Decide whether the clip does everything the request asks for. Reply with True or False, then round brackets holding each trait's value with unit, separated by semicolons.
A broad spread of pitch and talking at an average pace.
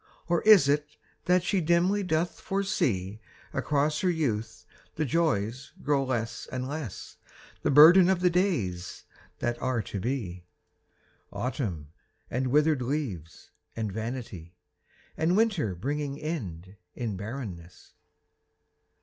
False (7.4 semitones; 120 wpm)